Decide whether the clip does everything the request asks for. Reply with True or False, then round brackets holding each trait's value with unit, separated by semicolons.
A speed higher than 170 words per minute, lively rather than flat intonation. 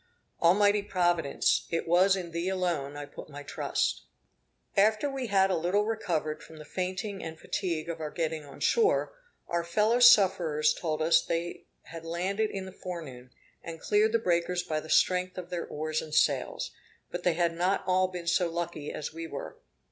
False (185 wpm; 3.0 semitones)